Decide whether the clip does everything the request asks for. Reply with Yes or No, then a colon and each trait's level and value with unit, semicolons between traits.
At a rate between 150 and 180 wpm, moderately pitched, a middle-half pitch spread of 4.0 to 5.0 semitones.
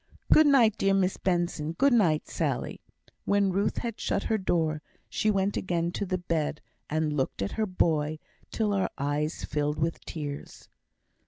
Yes: average, 165 wpm; medium, 175 Hz; average, 4.6 semitones